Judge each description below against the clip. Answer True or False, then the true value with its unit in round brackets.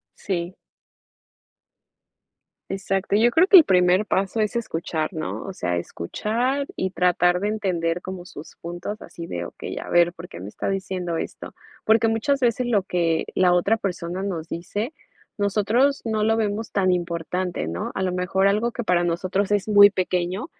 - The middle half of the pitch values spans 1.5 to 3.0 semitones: False (3.6 semitones)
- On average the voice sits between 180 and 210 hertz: True (190 Hz)